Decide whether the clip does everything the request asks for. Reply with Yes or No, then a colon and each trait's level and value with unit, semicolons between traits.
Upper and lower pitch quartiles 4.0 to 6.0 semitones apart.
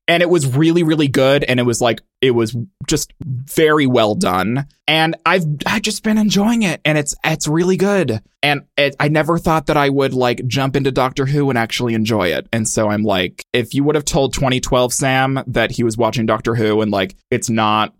Yes: average, 4.7 semitones